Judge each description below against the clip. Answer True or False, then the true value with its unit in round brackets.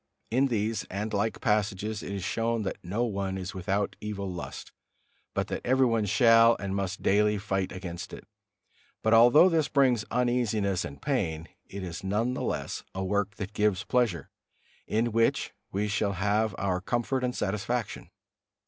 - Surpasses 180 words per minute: False (165 wpm)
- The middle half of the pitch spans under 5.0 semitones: True (3.0 semitones)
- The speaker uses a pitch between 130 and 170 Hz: False (105 Hz)